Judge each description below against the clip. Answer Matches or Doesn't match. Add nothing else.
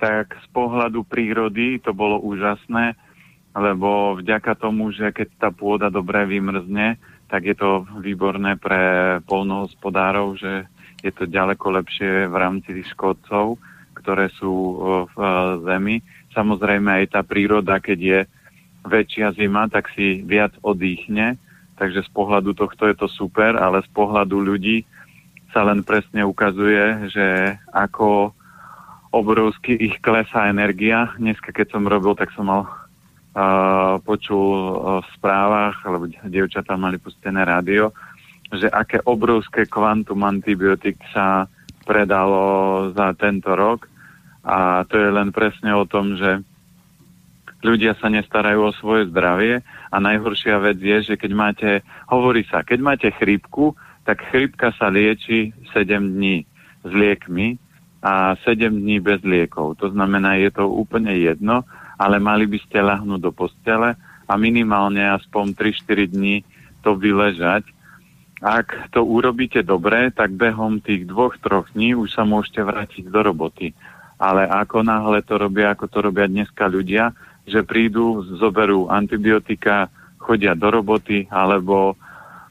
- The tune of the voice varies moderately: Doesn't match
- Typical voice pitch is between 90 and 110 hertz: Matches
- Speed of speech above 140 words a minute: Doesn't match